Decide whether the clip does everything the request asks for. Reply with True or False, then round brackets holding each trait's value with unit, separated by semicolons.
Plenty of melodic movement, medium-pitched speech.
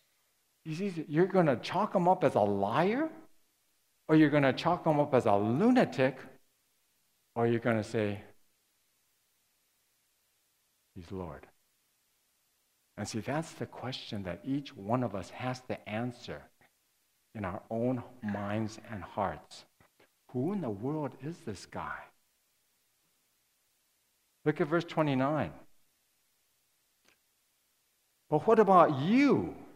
False (7.0 semitones; 125 Hz)